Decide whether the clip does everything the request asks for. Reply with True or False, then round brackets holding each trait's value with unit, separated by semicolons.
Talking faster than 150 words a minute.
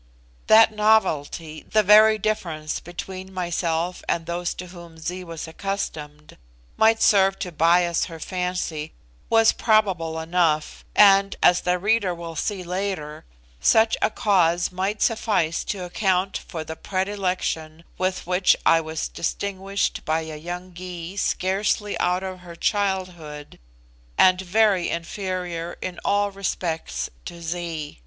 False (135 wpm)